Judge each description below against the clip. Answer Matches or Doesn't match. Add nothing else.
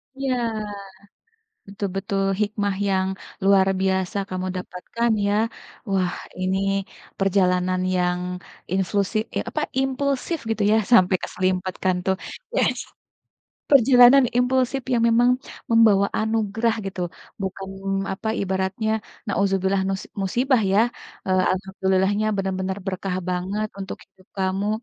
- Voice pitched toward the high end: Matches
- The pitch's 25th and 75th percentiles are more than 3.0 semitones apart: Doesn't match